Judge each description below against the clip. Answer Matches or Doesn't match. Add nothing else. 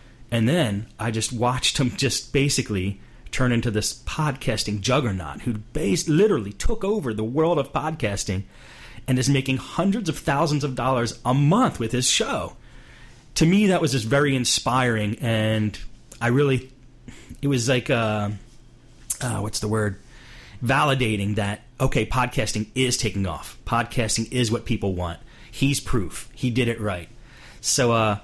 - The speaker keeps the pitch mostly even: Doesn't match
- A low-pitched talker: Matches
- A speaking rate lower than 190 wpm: Matches